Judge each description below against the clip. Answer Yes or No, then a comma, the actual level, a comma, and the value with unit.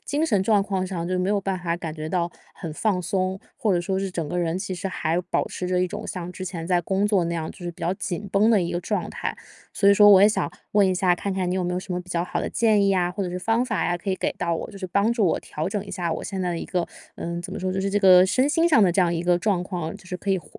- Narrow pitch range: Yes, narrow, 2.3 semitones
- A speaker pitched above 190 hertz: No, medium, 185 Hz